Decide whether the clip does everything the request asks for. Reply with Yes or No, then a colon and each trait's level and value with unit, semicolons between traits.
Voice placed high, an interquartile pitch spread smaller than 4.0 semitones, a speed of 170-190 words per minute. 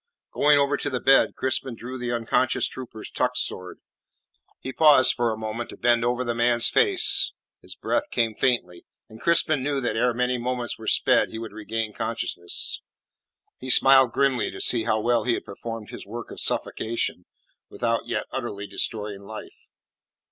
No: low, 120 Hz; average, 2.8 semitones; average, 175 wpm